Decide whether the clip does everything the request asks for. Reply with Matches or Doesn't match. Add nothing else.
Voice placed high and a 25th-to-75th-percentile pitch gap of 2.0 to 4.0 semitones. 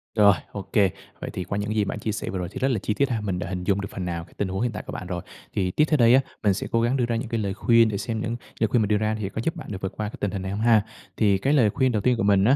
Doesn't match